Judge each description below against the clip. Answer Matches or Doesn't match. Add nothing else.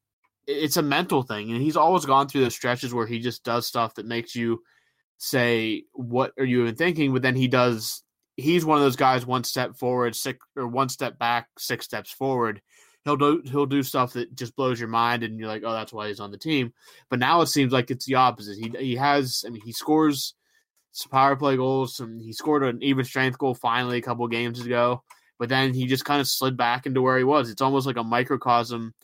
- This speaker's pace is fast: Matches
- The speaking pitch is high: Doesn't match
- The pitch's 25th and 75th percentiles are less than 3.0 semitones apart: Matches